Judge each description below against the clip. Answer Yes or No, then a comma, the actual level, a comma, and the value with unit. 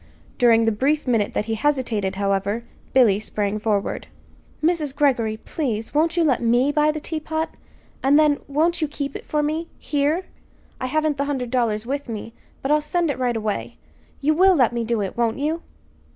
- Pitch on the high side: Yes, very high, 270 Hz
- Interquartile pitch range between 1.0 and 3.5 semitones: No, average, 5.2 semitones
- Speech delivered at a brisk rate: No, average, 190 wpm